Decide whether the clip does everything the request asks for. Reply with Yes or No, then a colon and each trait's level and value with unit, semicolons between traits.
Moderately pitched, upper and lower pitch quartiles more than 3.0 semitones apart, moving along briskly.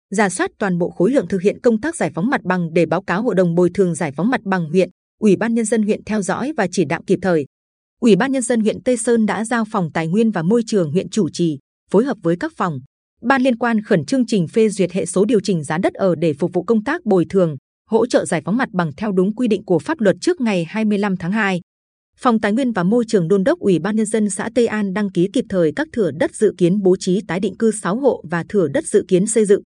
No: high, 200 Hz; average, 4.0 semitones; fast, 280 wpm